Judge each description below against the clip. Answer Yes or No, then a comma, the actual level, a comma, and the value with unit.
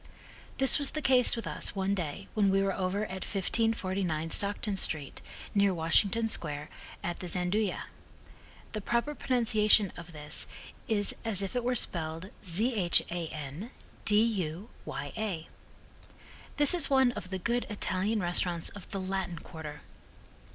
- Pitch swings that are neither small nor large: Yes, average, 4.3 semitones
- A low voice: No, high, 195 Hz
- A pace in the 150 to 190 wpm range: No, average, 140 wpm